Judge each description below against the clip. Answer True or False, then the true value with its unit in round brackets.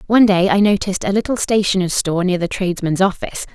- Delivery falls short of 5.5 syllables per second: False (6.9 syllables/s)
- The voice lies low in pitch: False (190 Hz)